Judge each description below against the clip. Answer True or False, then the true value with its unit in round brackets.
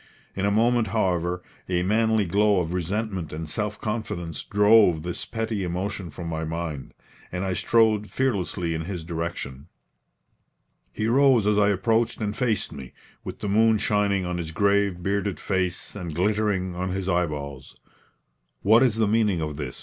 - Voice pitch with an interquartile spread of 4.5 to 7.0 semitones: False (3.7 semitones)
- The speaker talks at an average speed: True (165 wpm)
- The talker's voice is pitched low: True (95 Hz)